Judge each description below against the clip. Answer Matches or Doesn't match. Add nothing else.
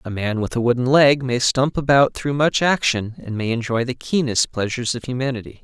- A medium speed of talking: Doesn't match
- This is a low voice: Matches